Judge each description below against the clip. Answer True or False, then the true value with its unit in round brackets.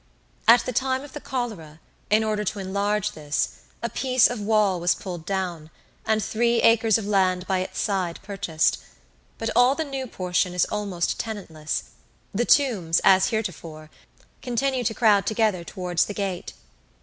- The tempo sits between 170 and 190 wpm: False (160 wpm)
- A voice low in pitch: False (205 Hz)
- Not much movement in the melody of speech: False (4.1 semitones)